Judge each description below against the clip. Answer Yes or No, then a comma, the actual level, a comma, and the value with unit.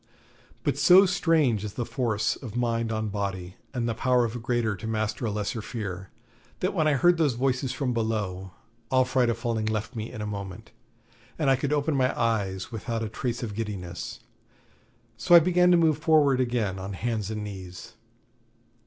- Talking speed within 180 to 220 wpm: Yes, average, 190 wpm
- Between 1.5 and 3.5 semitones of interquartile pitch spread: No, average, 3.9 semitones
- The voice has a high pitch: No, low, 115 Hz